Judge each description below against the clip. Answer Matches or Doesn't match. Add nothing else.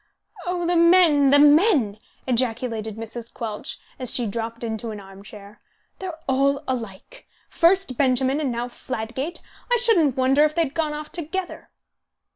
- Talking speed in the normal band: Matches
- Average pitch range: Doesn't match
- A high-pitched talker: Matches